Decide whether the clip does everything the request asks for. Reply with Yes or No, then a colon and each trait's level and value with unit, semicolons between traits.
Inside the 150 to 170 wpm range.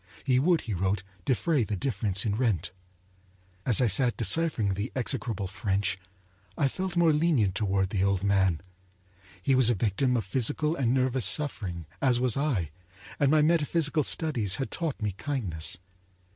Yes: average, 160 wpm